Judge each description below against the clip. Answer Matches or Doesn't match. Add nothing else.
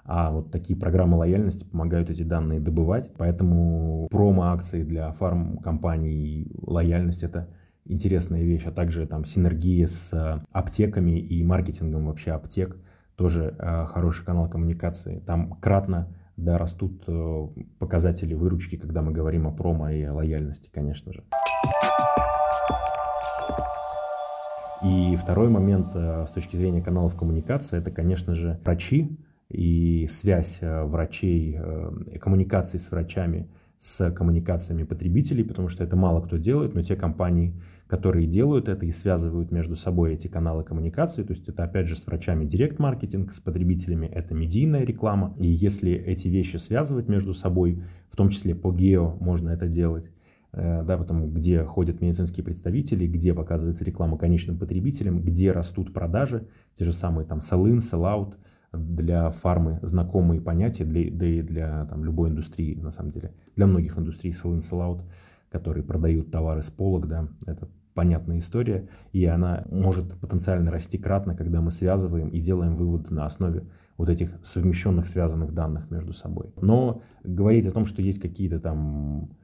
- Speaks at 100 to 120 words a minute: Doesn't match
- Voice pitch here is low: Matches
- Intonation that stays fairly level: Matches